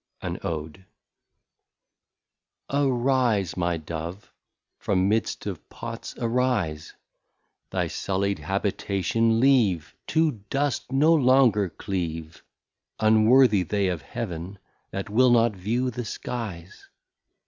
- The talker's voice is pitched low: Yes, low, 105 Hz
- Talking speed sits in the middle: No, slow, 100 wpm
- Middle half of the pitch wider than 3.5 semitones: Yes, average, 5.2 semitones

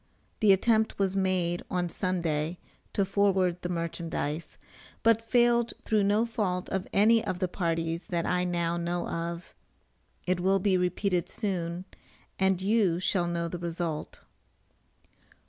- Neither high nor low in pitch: Yes, medium, 180 Hz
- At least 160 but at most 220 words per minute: No, average, 140 wpm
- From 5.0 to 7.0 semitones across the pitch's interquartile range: No, narrow, 2.6 semitones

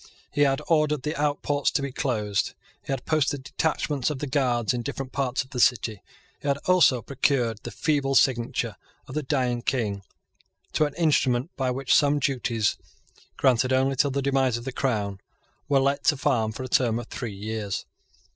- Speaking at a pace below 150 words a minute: No, average, 185 wpm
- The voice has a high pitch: No, low, 130 Hz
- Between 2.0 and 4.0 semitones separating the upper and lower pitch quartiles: Yes, average, 3.1 semitones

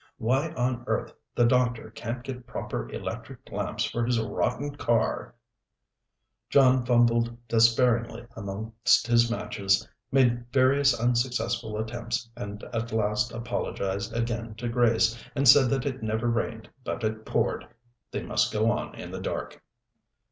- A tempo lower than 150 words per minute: Yes, average, 140 wpm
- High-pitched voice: No, low, 120 Hz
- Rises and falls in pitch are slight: Yes, narrow, 1.7 semitones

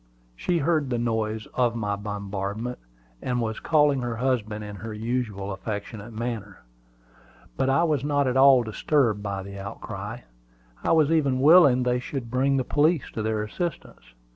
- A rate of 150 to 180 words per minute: Yes, average, 165 wpm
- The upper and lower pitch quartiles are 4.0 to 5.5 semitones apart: Yes, average, 4.4 semitones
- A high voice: No, low, 120 Hz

